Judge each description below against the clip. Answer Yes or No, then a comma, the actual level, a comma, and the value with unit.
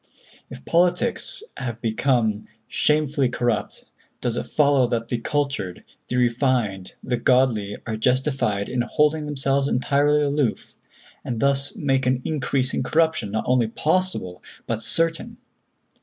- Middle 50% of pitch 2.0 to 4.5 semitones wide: Yes, average, 4.0 semitones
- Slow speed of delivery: Yes, slow, 130 wpm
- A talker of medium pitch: No, low, 130 Hz